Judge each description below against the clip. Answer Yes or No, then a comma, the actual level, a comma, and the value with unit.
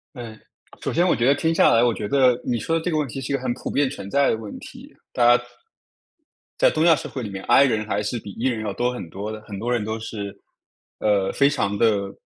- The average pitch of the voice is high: No, low, 120 Hz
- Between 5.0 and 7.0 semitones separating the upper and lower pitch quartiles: No, average, 4.4 semitones